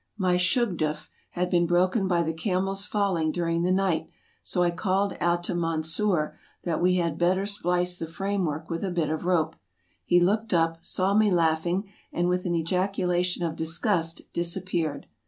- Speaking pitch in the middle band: Yes, medium, 175 Hz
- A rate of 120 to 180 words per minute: Yes, average, 175 wpm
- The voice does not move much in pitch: Yes, narrow, 2.3 semitones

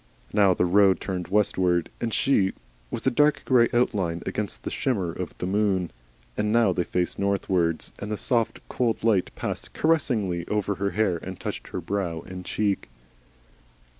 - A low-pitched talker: Yes, low, 100 Hz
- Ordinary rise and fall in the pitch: Yes, average, 3.0 semitones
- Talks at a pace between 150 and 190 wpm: Yes, average, 165 wpm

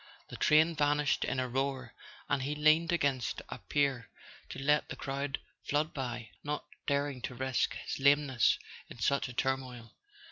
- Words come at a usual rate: Yes, average, 170 wpm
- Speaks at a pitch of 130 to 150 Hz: Yes, medium, 140 Hz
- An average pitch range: No, narrow, 2.2 semitones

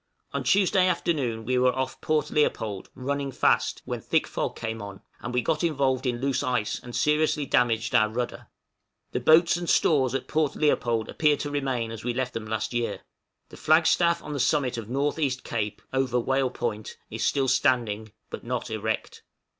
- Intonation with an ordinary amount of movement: Yes, average, 3.9 semitones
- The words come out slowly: No, average, 190 wpm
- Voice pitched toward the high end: No, low, 130 Hz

